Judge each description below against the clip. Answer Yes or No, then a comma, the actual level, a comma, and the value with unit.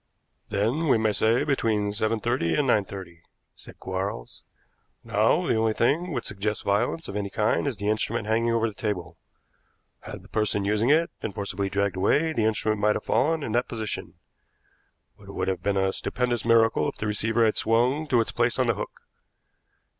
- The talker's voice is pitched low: Yes, low, 110 Hz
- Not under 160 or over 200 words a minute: Yes, average, 195 wpm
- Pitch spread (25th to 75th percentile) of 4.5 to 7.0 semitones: No, average, 2.8 semitones